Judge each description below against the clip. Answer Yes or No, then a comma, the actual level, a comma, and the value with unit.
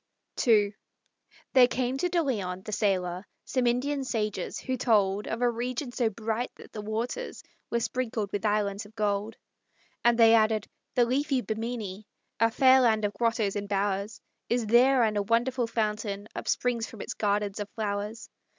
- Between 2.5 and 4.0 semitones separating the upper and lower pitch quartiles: Yes, average, 2.9 semitones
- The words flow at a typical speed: Yes, average, 170 wpm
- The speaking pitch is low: No, high, 225 Hz